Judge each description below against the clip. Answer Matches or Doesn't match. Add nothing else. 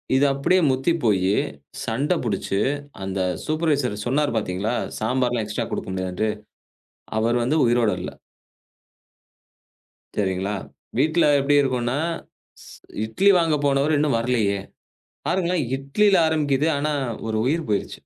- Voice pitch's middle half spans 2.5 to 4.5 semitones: Doesn't match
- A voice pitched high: Doesn't match